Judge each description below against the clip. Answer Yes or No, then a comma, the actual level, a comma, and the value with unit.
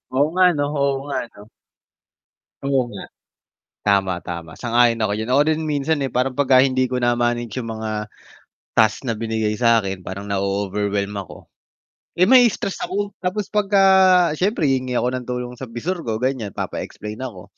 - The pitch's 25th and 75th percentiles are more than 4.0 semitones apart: Yes, average, 4.5 semitones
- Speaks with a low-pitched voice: Yes, low, 120 Hz